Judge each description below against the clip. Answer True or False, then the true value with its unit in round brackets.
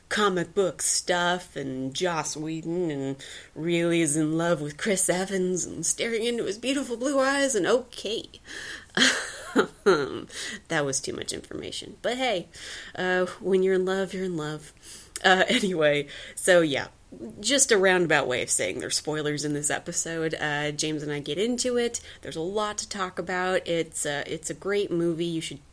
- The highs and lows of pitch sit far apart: False (4.0 semitones)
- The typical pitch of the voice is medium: True (170 Hz)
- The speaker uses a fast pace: False (175 wpm)